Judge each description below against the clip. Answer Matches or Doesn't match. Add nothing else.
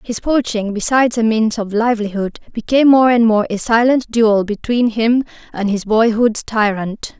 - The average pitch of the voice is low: Doesn't match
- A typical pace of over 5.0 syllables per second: Doesn't match